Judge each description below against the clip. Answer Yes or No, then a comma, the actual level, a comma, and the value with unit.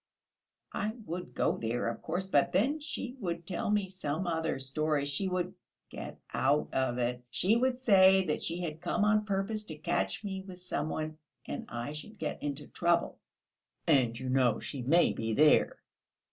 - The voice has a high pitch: No, medium, 170 Hz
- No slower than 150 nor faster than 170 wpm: No, average, 180 wpm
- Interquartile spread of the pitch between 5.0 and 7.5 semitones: Yes, wide, 5.5 semitones